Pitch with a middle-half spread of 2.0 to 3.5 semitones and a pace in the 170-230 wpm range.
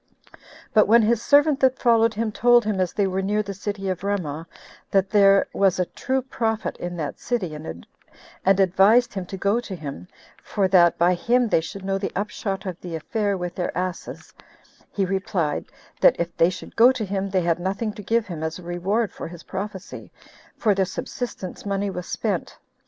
Yes: average, 3.2 semitones; average, 195 wpm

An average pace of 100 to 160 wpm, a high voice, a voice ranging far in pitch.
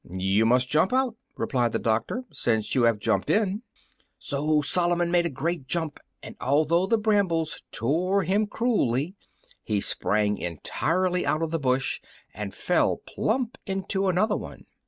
No: average, 155 wpm; medium, 160 Hz; wide, 7.7 semitones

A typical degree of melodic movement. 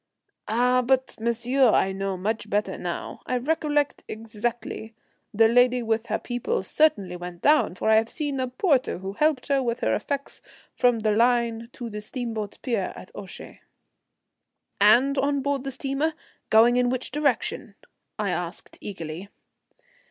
Yes: average, 3.8 semitones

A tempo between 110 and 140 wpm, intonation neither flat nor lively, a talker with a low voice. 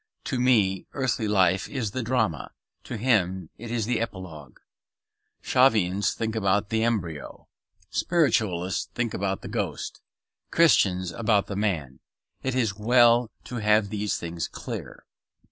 Yes: slow, 135 wpm; average, 4.0 semitones; low, 105 Hz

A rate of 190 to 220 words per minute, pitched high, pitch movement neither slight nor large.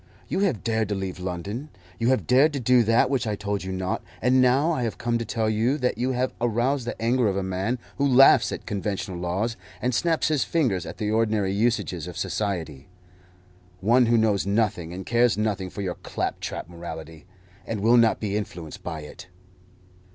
No: average, 200 wpm; low, 110 Hz; average, 4.5 semitones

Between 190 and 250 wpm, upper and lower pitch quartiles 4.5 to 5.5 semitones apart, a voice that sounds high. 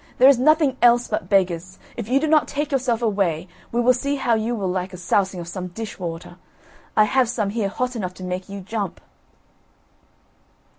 Yes: average, 200 wpm; average, 5.2 semitones; high, 215 Hz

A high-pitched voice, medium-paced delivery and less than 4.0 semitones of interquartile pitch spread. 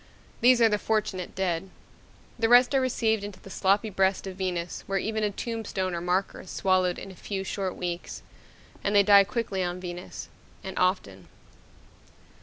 Yes: high, 195 Hz; average, 175 wpm; average, 2.7 semitones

